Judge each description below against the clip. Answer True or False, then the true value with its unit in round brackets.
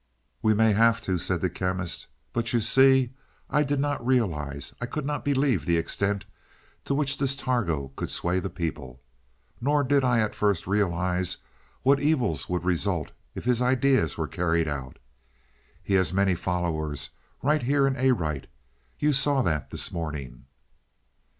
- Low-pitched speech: True (105 Hz)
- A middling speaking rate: True (160 wpm)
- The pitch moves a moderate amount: False (7.7 semitones)